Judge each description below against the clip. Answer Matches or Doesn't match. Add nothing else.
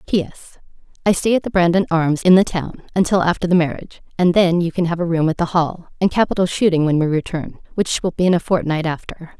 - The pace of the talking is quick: Matches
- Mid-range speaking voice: Matches